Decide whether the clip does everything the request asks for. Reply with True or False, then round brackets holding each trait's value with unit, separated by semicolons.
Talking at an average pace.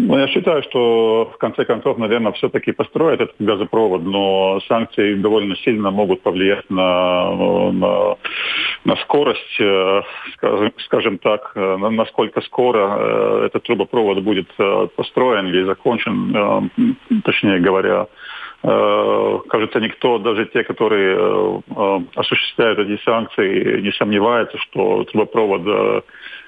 False (100 wpm)